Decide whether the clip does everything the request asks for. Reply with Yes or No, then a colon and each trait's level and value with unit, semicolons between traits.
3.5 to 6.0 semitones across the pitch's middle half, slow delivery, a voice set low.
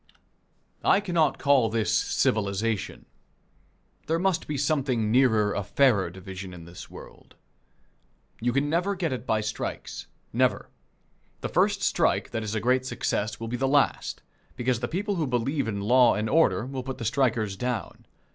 No: average, 4.5 semitones; average, 165 wpm; low, 120 Hz